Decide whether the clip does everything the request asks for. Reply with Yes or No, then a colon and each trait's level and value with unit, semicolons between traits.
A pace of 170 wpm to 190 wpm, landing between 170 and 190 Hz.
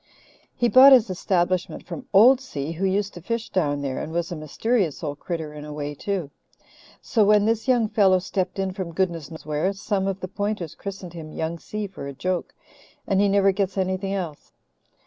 No: fast, 205 wpm; medium, 185 Hz